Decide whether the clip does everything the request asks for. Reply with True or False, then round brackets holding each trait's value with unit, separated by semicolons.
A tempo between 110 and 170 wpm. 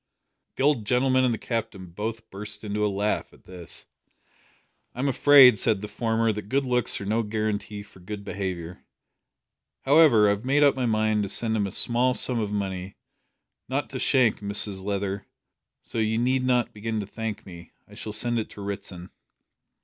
False (185 wpm)